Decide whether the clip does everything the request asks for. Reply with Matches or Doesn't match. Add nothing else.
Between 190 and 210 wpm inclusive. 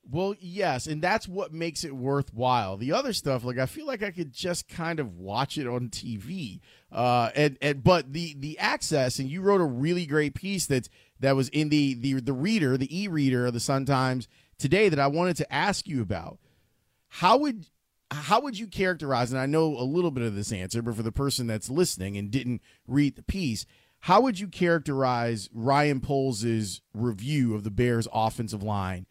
Matches